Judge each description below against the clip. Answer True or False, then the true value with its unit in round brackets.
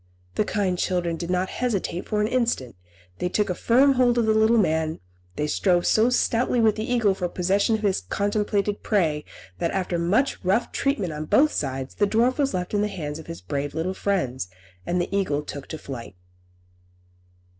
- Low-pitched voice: False (190 Hz)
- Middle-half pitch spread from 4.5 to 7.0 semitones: True (5.0 semitones)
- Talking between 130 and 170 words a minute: False (195 wpm)